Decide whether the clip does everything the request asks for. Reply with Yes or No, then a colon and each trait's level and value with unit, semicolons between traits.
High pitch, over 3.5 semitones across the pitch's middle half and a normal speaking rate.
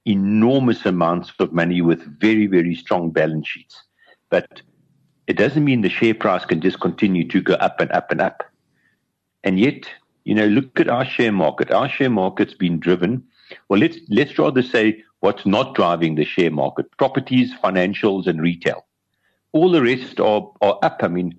No: very low, 95 Hz; average, 4.9 semitones; average, 180 wpm